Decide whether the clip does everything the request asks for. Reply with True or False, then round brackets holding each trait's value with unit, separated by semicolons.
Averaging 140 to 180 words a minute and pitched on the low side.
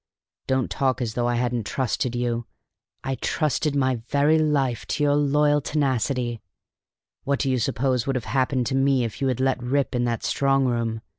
False (195 wpm; 130 Hz)